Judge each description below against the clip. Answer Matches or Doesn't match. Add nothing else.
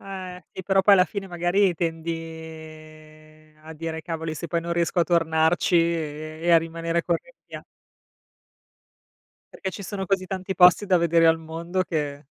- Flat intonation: Matches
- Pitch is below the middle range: Doesn't match